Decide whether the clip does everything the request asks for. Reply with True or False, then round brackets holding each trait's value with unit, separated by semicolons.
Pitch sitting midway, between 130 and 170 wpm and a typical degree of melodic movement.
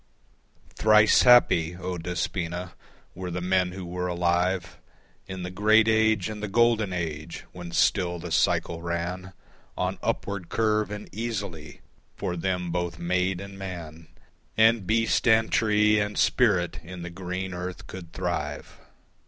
False (90 Hz; 145 wpm; 3.2 semitones)